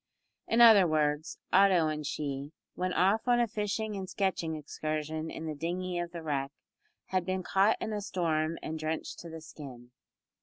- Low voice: No, medium, 165 Hz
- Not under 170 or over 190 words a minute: Yes, average, 180 wpm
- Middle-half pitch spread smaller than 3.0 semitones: No, average, 3.8 semitones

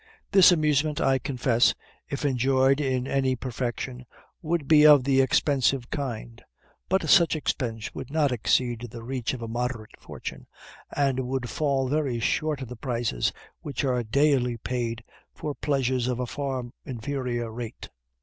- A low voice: Yes, low, 130 Hz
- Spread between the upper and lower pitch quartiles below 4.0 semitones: Yes, average, 2.8 semitones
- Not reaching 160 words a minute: Yes, average, 150 wpm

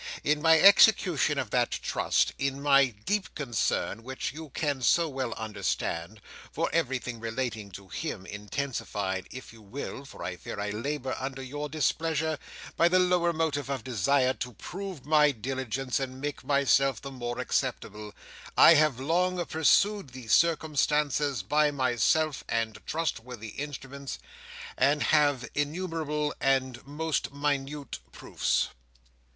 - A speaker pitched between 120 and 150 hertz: Yes, medium, 140 Hz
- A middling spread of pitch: Yes, average, 3.7 semitones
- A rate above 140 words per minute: No, slow, 135 wpm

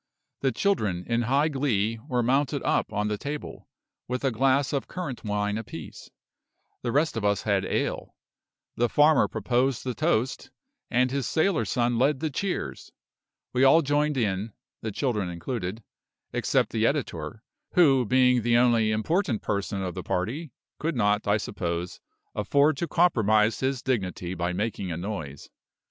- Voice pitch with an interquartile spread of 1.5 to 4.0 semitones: No, average, 5.1 semitones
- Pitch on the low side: Yes, low, 120 Hz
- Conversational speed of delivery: Yes, average, 155 wpm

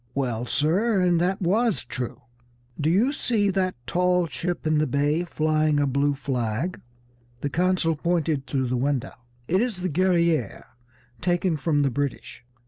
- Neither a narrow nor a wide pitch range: Yes, average, 4.3 semitones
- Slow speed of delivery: No, average, 155 wpm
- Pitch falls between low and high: Yes, medium, 160 Hz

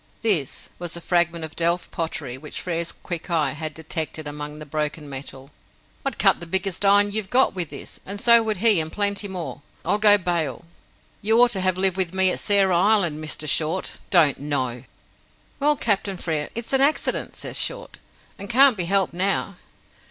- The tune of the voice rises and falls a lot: No, average, 4.4 semitones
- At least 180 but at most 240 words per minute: Yes, average, 190 wpm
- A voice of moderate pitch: Yes, medium, 175 Hz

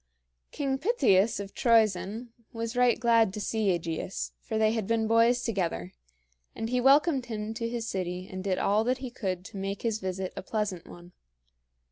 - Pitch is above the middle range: Yes, high, 220 Hz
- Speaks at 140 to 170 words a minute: No, average, 180 wpm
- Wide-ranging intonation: No, average, 3.7 semitones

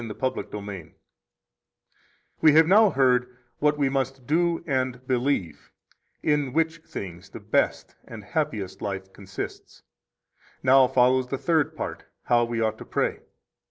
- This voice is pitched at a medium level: No, low, 130 Hz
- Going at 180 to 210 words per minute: No, average, 145 wpm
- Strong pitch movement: No, average, 4.9 semitones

